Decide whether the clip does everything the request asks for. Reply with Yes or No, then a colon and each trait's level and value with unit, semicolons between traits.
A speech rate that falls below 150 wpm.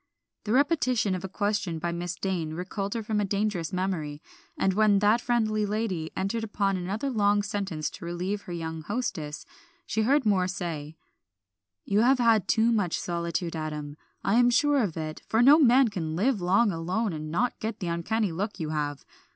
No: average, 185 wpm